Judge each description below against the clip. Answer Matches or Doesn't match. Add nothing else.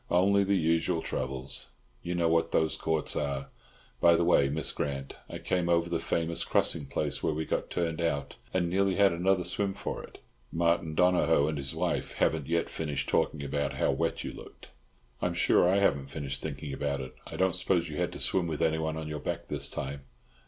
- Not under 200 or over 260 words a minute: Matches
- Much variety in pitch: Doesn't match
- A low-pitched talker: Matches